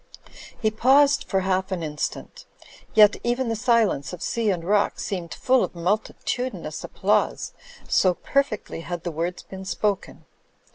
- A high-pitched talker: Yes, high, 200 Hz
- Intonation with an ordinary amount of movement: Yes, average, 4.6 semitones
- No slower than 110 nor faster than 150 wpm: Yes, average, 145 wpm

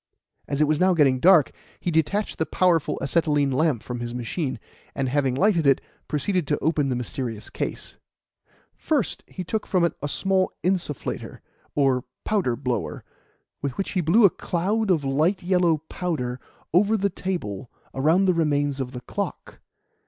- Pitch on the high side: No, medium, 155 Hz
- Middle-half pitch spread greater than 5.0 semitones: Yes, wide, 5.5 semitones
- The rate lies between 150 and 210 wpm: Yes, average, 165 wpm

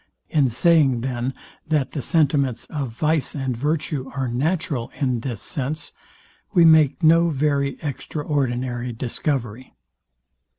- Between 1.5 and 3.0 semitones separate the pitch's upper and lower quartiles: No, average, 3.5 semitones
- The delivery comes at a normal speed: No, slow, 120 wpm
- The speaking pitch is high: No, medium, 140 Hz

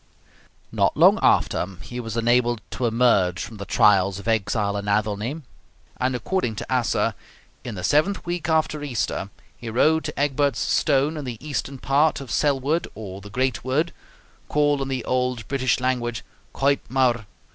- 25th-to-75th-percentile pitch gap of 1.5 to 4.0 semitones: No, average, 4.5 semitones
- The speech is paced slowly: No, average, 165 wpm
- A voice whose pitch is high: No, low, 125 Hz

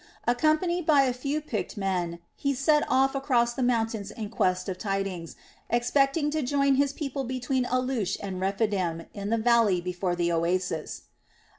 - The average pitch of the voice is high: Yes, high, 235 Hz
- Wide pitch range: Yes, wide, 6.1 semitones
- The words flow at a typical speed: Yes, average, 160 wpm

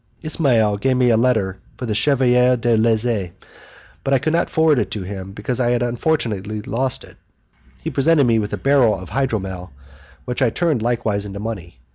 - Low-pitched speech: Yes, low, 120 Hz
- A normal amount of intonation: Yes, average, 4.0 semitones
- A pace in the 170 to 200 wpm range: Yes, average, 185 wpm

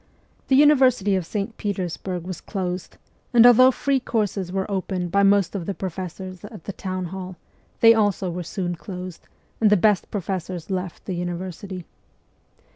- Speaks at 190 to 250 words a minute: No, average, 160 wpm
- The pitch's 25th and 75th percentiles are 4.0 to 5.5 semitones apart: No, narrow, 2.5 semitones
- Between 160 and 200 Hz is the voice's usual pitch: Yes, high, 190 Hz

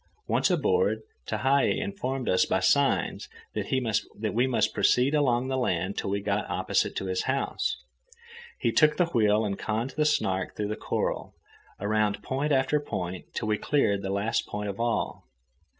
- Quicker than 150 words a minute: Yes, average, 165 wpm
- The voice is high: No, low, 115 Hz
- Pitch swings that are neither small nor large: Yes, average, 4.8 semitones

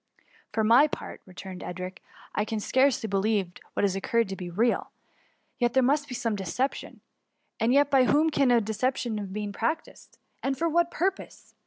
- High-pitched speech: Yes, high, 230 Hz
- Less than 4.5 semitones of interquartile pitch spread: No, average, 5.0 semitones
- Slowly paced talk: No, average, 175 wpm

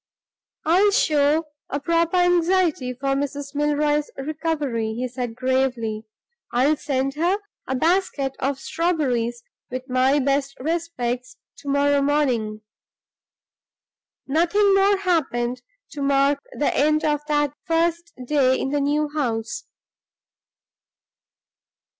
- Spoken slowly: Yes, slow, 110 wpm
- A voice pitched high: Yes, very high, 285 Hz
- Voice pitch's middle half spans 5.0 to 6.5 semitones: No, average, 3.7 semitones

